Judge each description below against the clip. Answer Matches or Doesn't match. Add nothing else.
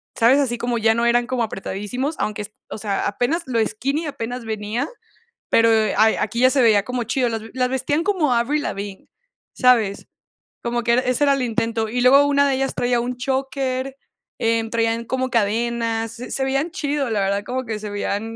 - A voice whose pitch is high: Matches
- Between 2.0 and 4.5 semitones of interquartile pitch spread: Matches